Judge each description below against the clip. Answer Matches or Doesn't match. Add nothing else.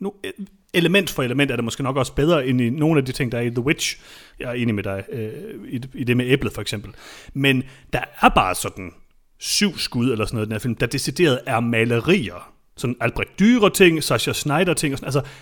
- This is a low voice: Matches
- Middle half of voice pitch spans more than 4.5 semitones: Matches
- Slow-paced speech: Doesn't match